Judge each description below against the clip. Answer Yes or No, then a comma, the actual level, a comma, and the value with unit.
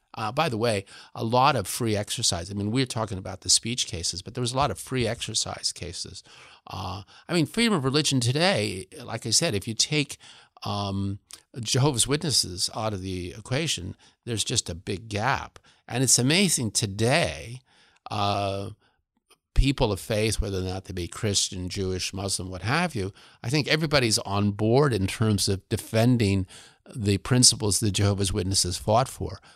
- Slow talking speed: No, average, 175 wpm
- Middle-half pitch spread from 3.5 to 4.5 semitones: Yes, average, 4.2 semitones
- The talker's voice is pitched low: Yes, low, 110 Hz